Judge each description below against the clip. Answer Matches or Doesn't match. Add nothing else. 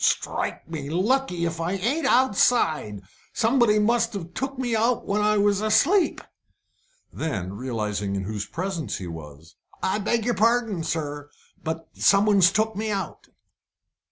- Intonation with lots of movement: Matches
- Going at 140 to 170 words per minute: Matches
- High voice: Matches